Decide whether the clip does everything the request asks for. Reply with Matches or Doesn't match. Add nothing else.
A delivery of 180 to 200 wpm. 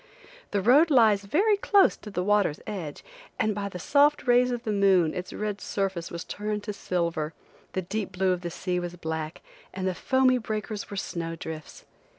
Matches